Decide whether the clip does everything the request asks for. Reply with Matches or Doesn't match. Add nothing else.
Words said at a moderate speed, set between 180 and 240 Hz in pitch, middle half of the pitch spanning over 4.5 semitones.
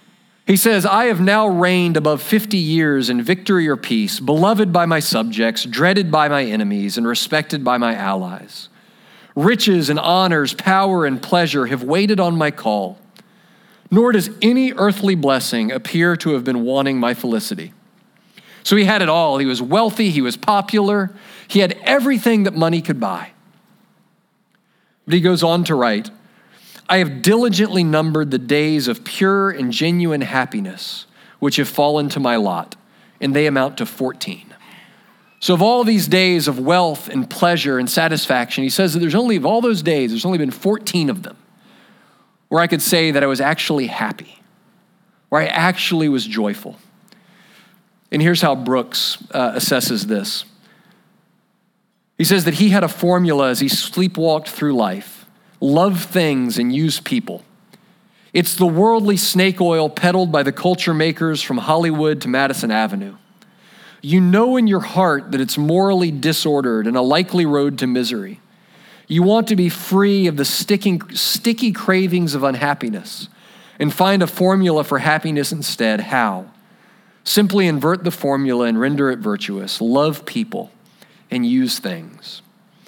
Matches